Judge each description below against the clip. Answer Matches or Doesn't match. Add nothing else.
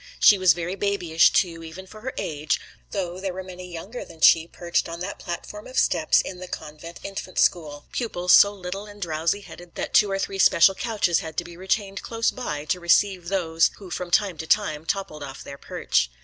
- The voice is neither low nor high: Matches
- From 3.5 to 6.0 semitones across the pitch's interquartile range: Doesn't match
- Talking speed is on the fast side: Matches